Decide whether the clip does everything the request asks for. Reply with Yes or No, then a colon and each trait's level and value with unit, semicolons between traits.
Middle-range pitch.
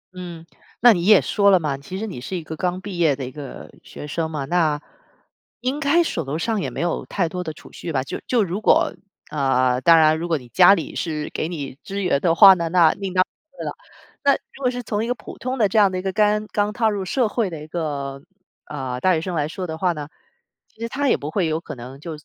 Yes: medium, 175 Hz